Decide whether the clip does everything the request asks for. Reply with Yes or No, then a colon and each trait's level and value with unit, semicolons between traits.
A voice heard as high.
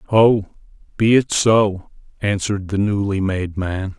No: low, 100 Hz